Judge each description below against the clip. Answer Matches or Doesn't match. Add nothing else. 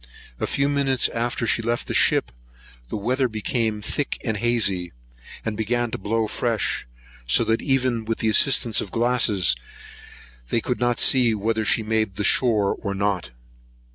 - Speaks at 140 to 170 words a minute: Matches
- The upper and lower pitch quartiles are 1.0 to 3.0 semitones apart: Matches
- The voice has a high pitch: Doesn't match